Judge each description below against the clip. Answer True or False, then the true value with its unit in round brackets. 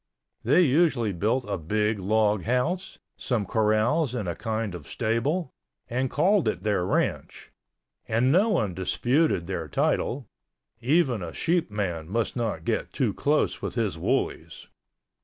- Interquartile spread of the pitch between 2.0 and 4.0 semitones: False (5.2 semitones)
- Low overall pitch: True (115 Hz)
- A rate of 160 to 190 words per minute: False (140 wpm)